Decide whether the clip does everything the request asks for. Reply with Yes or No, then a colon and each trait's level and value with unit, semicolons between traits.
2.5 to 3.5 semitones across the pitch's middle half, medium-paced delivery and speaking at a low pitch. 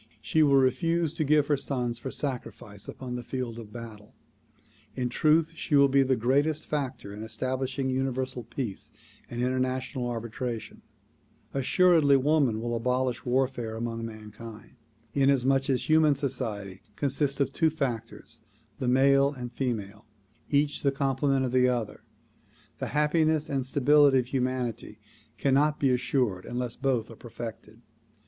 Yes: average, 2.9 semitones; average, 145 wpm; low, 130 Hz